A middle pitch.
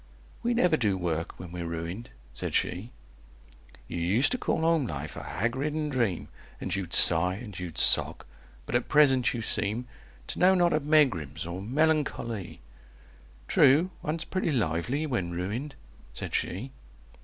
No: low, 115 Hz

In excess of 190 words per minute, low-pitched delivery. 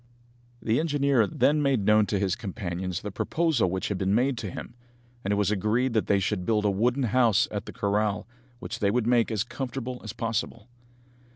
Yes: average, 200 wpm; low, 110 Hz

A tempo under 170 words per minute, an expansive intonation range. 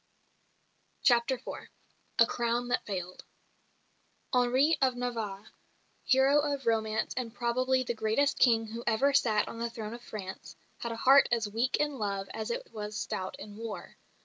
No: average, 160 wpm; average, 3.0 semitones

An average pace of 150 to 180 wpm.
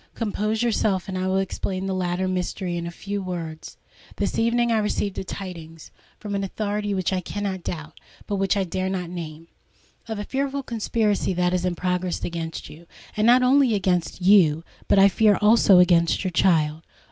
Yes: average, 170 wpm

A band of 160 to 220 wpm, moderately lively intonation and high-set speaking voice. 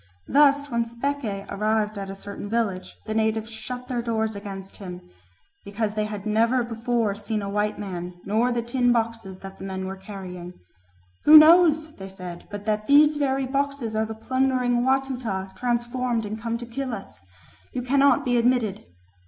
Yes: average, 175 wpm; average, 3.8 semitones; high, 225 Hz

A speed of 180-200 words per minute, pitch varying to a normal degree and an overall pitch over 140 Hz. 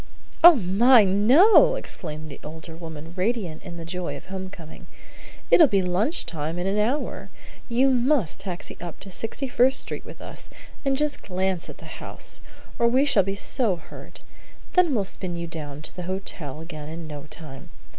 No: average, 185 wpm; wide, 6.5 semitones; medium, 185 Hz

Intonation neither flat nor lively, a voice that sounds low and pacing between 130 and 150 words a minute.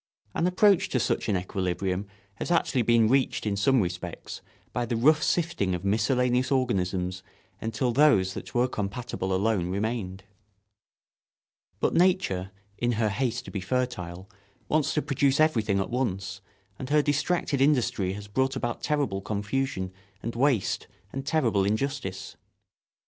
No: wide, 5.7 semitones; low, 115 Hz; average, 145 wpm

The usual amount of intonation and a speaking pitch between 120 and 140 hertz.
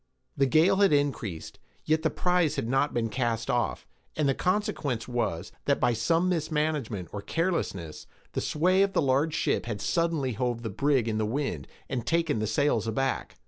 No: wide, 5.8 semitones; low, 135 Hz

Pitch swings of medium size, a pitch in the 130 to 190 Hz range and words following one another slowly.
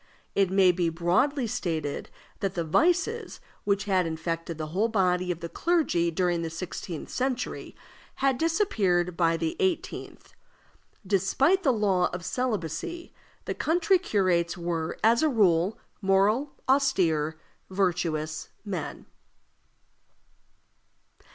No: wide, 6.7 semitones; medium, 185 Hz; slow, 120 wpm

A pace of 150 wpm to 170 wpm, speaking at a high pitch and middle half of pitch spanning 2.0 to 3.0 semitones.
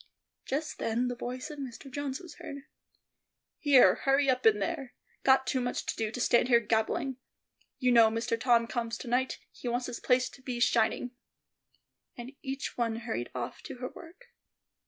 No: average, 180 wpm; very high, 250 Hz; narrow, 2.5 semitones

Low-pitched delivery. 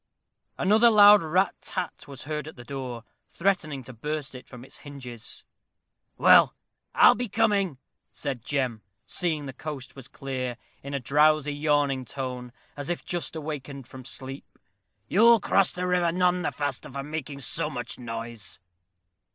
No: medium, 145 Hz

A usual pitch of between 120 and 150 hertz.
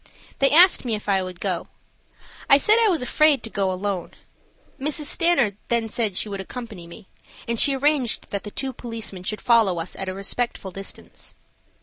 No: high, 225 Hz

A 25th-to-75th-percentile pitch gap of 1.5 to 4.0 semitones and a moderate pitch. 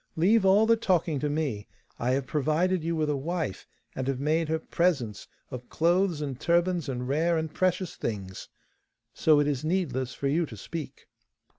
No: average, 4.4 semitones; medium, 155 Hz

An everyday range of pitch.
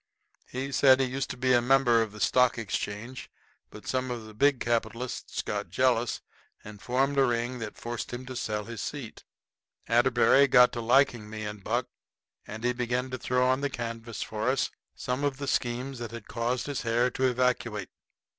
No: narrow, 2.1 semitones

